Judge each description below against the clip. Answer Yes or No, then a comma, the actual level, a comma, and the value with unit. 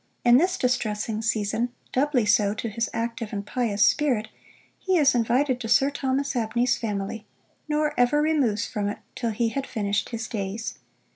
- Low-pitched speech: No, high, 230 Hz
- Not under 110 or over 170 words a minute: Yes, average, 165 wpm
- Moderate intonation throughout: Yes, average, 3.8 semitones